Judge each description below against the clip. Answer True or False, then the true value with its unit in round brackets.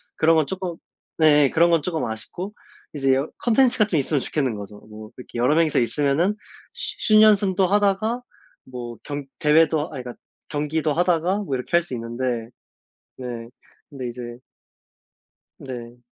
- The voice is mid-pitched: True (150 Hz)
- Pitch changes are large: True (6.1 semitones)